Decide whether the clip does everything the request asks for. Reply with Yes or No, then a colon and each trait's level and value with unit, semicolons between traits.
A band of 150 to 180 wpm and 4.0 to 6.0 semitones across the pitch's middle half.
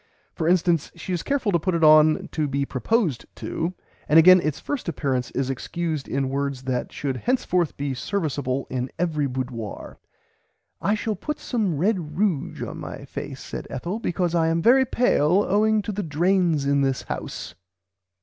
Yes: average, 175 wpm; wide, 5.5 semitones